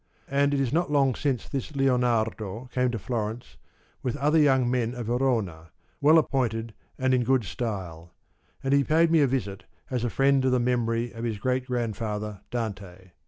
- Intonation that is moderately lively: Yes, average, 3.4 semitones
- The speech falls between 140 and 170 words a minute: No, average, 180 wpm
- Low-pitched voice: Yes, low, 125 Hz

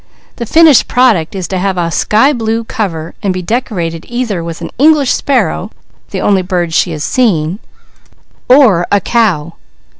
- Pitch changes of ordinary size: No, wide, 6.1 semitones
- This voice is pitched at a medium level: No, high, 200 Hz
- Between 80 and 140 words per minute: No, average, 160 wpm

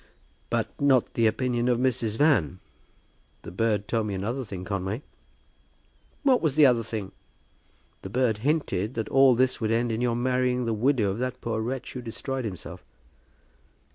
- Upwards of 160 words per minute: Yes, average, 170 wpm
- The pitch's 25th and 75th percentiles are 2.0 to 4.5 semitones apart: Yes, average, 3.0 semitones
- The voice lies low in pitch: Yes, low, 120 Hz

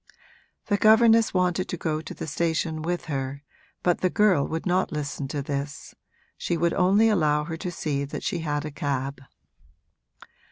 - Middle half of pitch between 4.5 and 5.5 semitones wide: No, average, 3.9 semitones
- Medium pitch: Yes, medium, 160 Hz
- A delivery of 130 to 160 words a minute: No, average, 170 wpm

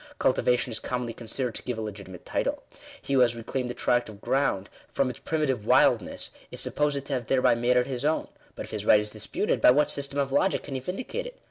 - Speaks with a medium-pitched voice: No, low, 125 Hz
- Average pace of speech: No, fast, 235 wpm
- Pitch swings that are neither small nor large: Yes, average, 3.3 semitones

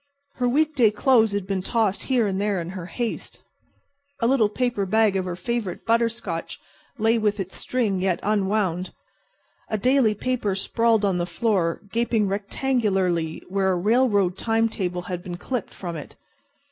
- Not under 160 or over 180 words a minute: Yes, average, 170 wpm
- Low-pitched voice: No, high, 205 Hz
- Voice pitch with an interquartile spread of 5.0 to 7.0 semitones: No, average, 3.8 semitones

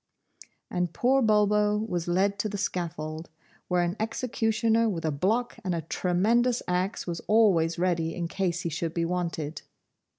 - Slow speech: No, average, 160 wpm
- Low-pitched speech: No, medium, 180 Hz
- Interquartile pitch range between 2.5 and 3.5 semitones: No, average, 4.2 semitones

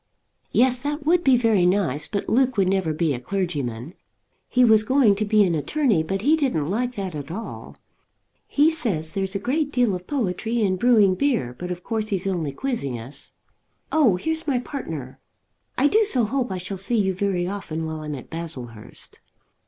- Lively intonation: Yes, wide, 7.1 semitones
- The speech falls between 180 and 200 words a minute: Yes, average, 190 wpm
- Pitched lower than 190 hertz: No, high, 200 Hz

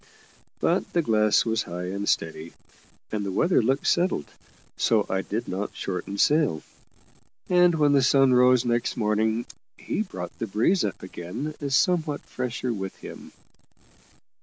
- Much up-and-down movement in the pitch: Yes, wide, 6.0 semitones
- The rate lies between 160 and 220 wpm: No, average, 145 wpm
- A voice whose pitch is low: Yes, low, 115 Hz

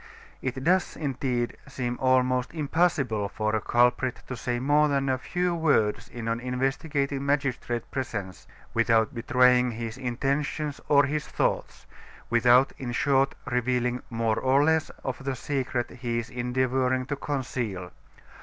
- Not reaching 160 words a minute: Yes, average, 140 wpm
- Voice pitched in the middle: No, low, 130 Hz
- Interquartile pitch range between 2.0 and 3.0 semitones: Yes, narrow, 2.4 semitones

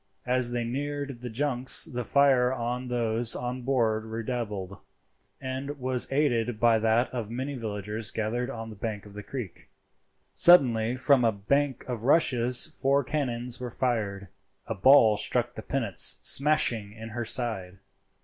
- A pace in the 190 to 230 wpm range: No, average, 150 wpm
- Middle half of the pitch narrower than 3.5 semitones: Yes, average, 2.8 semitones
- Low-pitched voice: Yes, low, 120 Hz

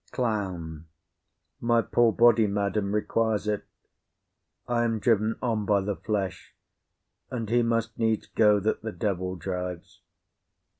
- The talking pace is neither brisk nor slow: No, slow, 130 wpm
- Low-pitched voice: Yes, low, 105 Hz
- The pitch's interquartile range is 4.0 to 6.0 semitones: No, narrow, 2.6 semitones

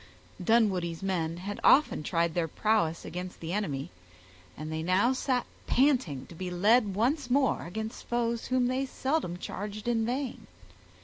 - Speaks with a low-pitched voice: No, high, 205 Hz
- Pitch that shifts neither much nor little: No, wide, 6.2 semitones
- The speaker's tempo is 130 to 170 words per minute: Yes, average, 150 wpm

